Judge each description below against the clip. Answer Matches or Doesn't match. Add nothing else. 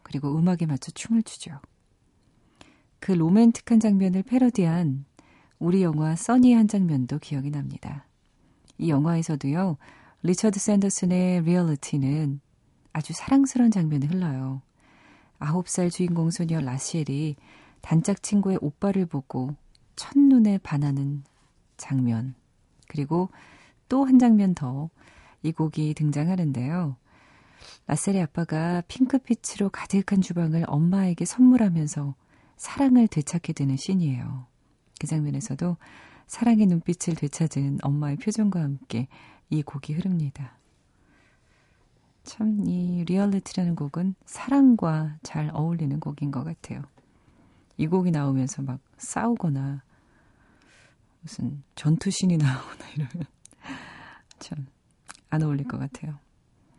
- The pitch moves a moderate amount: Matches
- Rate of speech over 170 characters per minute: Matches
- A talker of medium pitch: Matches